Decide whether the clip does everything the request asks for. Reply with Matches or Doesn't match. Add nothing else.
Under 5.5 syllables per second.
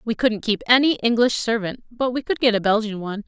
Doesn't match